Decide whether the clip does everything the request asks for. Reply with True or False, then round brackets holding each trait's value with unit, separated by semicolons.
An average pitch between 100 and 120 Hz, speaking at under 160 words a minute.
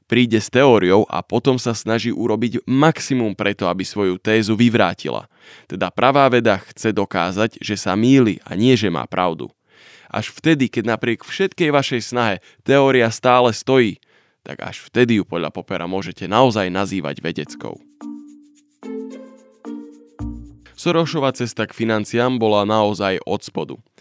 True (115 Hz; 135 wpm)